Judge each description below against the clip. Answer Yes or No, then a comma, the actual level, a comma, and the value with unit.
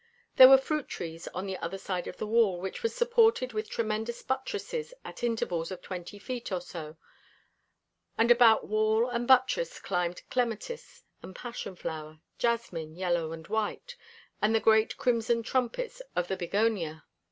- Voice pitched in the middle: No, high, 220 Hz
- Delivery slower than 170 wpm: Yes, average, 160 wpm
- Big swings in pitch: Yes, wide, 5.7 semitones